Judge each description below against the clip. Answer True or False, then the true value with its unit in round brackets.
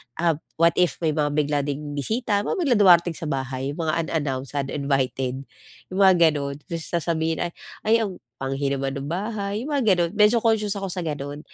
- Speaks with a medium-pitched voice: True (160 Hz)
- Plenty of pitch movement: True (5.8 semitones)